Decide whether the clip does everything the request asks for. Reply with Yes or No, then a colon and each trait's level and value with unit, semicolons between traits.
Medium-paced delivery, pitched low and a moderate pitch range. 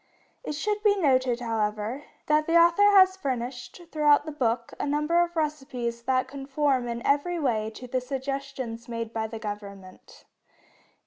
No: average, 155 wpm; very high, 265 Hz; average, 4.4 semitones